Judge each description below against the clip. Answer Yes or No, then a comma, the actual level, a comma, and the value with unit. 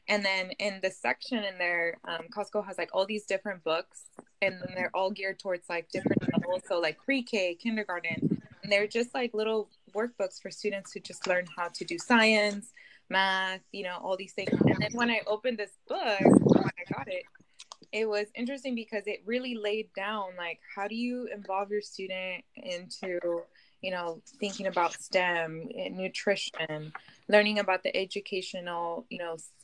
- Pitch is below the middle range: No, high, 195 Hz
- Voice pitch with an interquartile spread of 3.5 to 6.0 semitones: No, average, 3.0 semitones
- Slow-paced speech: No, average, 180 wpm